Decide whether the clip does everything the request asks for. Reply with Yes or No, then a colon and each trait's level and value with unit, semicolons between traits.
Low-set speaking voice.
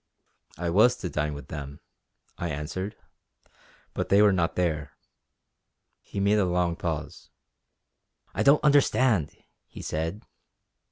Yes: very low, 90 Hz